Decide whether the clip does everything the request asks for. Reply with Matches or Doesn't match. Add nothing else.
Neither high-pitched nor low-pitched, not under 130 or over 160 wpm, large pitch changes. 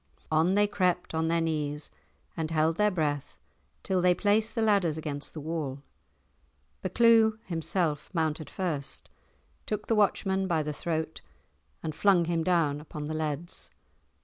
Doesn't match